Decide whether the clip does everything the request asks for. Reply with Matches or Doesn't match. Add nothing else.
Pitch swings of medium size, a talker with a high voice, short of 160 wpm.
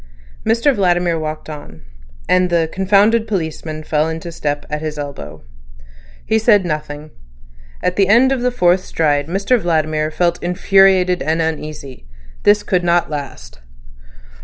Doesn't match